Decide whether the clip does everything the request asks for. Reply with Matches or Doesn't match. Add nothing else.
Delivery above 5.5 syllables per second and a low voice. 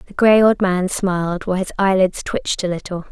Doesn't match